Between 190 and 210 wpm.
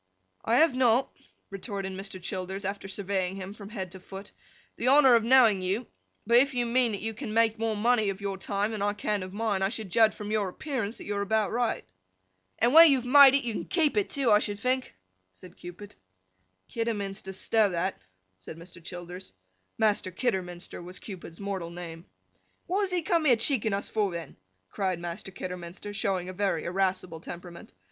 Yes: average, 195 wpm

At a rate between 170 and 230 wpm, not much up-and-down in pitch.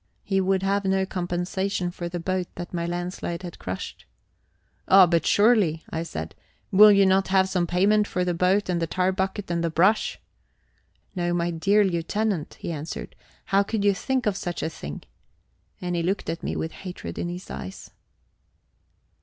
Yes: average, 180 wpm; narrow, 2.2 semitones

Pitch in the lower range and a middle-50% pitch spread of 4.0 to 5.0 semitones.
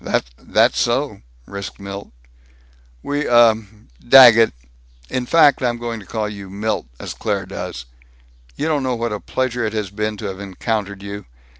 No: low, 110 Hz; average, 3.1 semitones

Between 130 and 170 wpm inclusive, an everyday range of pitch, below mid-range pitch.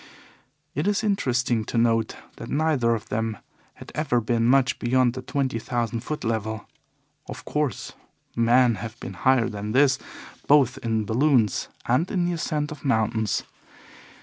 Yes: average, 150 wpm; average, 3.8 semitones; low, 120 Hz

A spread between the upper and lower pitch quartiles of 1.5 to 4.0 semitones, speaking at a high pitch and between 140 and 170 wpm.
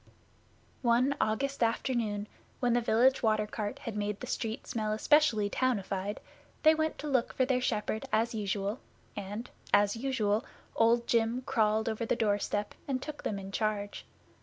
Yes: average, 3.2 semitones; high, 225 Hz; average, 160 wpm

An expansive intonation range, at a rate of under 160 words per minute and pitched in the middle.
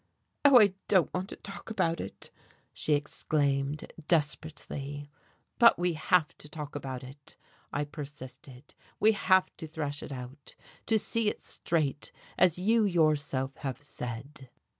No: average, 4.4 semitones; average, 140 wpm; medium, 150 Hz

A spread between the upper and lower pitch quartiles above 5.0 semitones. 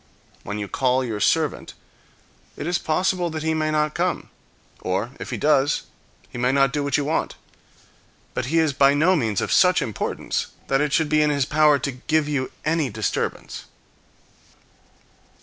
No: average, 3.2 semitones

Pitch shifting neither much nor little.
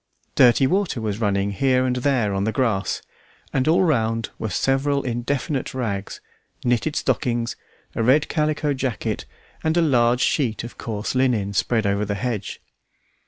Yes: average, 3.8 semitones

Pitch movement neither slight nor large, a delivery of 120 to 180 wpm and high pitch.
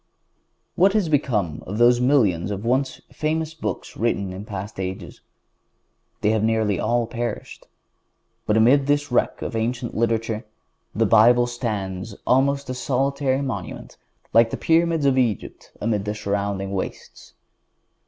No: average, 4.5 semitones; average, 140 wpm; low, 115 Hz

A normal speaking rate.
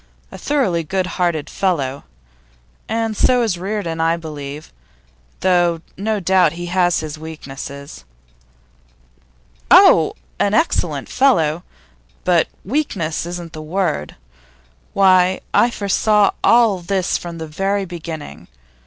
No: slow, 115 wpm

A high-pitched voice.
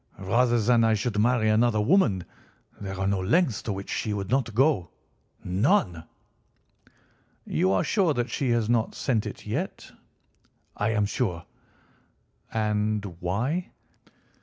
No: low, 110 Hz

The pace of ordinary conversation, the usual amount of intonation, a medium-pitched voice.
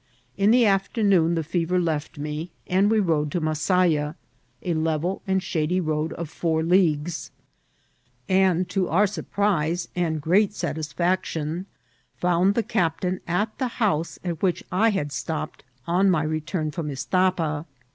Yes: average, 145 wpm; average, 3.2 semitones; medium, 170 Hz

